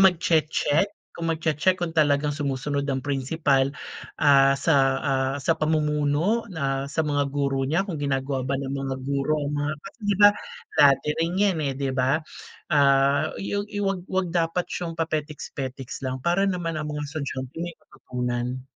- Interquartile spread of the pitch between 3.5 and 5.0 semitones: No, average, 3.1 semitones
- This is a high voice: No, medium, 145 Hz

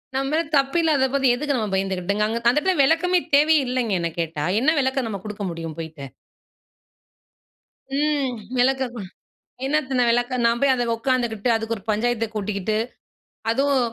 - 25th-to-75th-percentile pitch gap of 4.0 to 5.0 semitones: Yes, average, 4.5 semitones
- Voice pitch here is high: Yes, high, 245 Hz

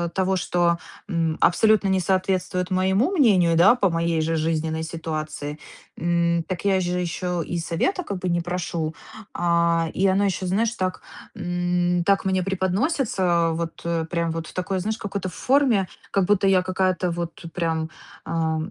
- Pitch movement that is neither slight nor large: No, narrow, 2.3 semitones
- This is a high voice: No, medium, 180 Hz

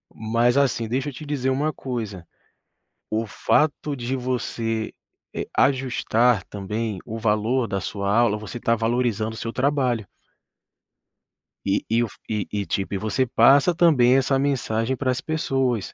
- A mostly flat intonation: No, average, 3.3 semitones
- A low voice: Yes, low, 120 Hz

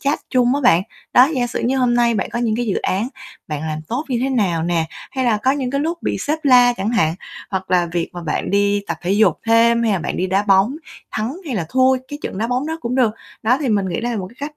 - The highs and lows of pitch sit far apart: No, average, 5.0 semitones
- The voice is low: No, high, 230 Hz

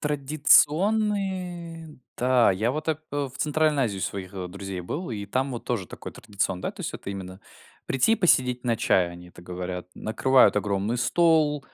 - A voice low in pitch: Yes, low, 125 Hz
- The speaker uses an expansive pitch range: Yes, wide, 7.9 semitones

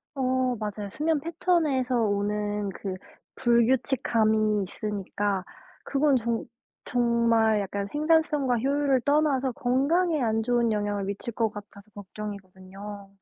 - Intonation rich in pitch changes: No, average, 4.4 semitones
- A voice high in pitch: Yes, high, 230 Hz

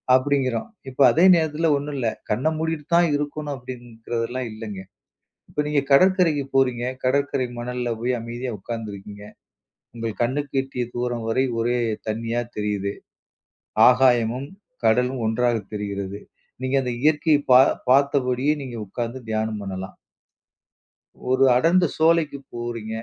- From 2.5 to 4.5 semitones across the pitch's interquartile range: Yes, average, 3.7 semitones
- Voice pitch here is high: No, low, 125 Hz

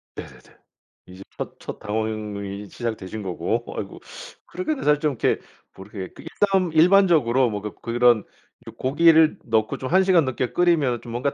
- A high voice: No, low, 120 Hz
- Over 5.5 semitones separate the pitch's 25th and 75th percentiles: Yes, wide, 7.2 semitones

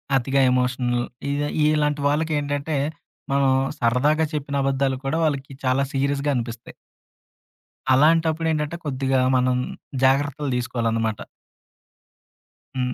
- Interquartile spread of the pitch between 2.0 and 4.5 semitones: Yes, narrow, 2.6 semitones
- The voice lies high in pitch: No, low, 135 Hz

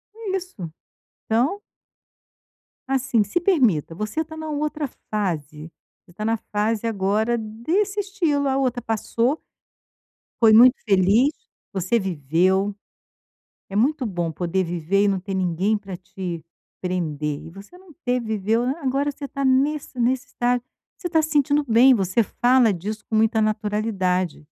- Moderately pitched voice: No, high, 220 Hz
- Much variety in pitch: Yes, wide, 6.2 semitones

